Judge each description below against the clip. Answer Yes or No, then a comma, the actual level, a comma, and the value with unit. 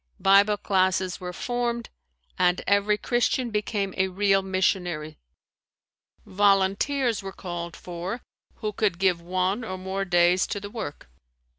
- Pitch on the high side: Yes, high, 195 Hz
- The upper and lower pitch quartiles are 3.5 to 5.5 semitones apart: No, narrow, 2.4 semitones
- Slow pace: Yes, slow, 130 wpm